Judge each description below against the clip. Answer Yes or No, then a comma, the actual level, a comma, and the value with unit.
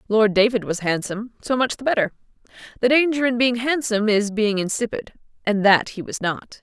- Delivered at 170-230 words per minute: Yes, average, 190 wpm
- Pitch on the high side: Yes, high, 220 Hz